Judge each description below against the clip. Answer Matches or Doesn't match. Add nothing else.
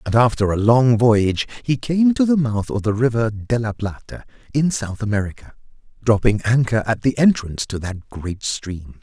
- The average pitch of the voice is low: Matches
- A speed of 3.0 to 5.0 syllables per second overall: Matches